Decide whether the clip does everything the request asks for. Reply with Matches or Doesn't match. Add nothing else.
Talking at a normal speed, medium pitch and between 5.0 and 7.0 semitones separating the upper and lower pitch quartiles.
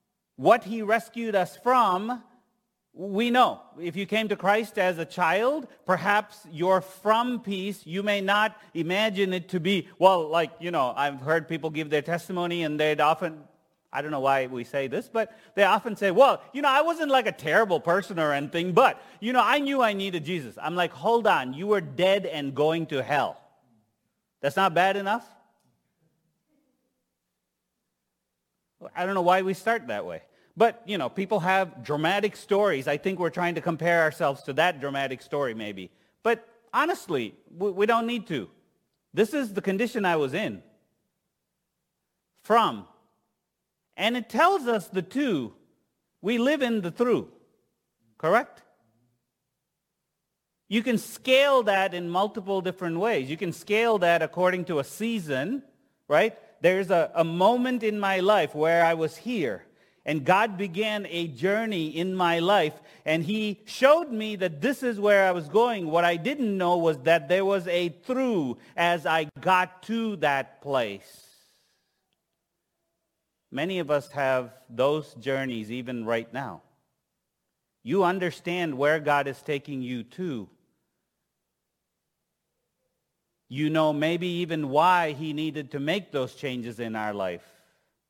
Matches